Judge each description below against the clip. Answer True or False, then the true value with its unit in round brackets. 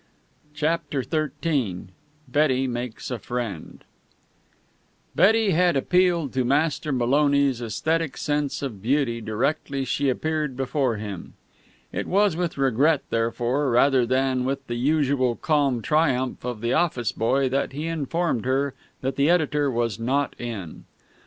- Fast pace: False (135 wpm)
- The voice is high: False (135 Hz)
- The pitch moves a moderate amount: True (3.9 semitones)